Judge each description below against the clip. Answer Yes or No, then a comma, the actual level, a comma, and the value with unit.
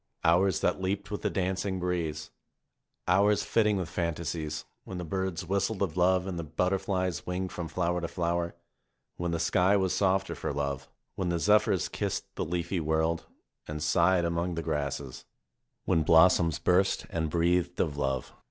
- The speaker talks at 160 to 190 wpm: Yes, average, 175 wpm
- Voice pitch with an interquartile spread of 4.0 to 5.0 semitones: No, narrow, 2.6 semitones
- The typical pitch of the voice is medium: No, very low, 85 Hz